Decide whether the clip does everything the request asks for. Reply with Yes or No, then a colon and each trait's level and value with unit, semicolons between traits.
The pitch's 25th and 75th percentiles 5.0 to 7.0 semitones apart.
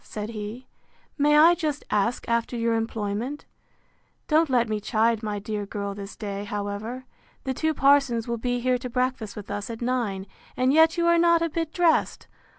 Yes: average, 5.3 semitones